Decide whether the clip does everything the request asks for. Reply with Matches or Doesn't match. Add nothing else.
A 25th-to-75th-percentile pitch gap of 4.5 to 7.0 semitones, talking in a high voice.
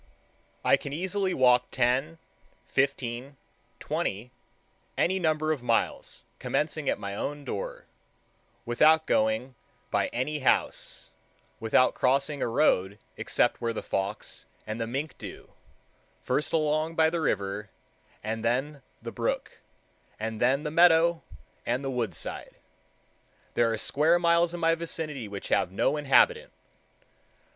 Doesn't match